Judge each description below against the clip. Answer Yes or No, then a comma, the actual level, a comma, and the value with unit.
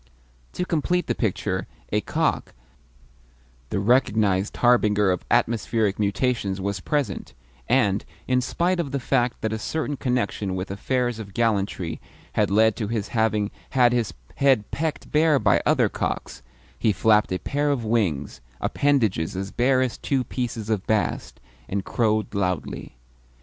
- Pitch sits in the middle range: No, low, 110 Hz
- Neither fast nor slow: Yes, average, 150 wpm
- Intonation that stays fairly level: No, average, 4.2 semitones